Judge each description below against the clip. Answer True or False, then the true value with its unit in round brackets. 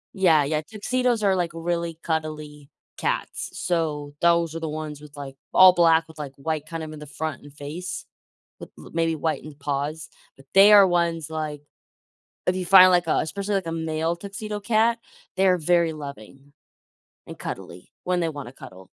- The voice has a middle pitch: True (160 Hz)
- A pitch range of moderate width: True (3.1 semitones)